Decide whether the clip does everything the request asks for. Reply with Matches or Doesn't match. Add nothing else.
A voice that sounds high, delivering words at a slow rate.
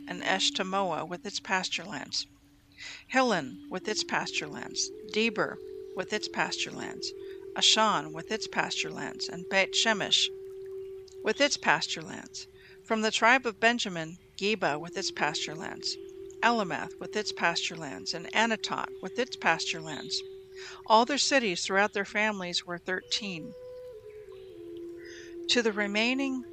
Matches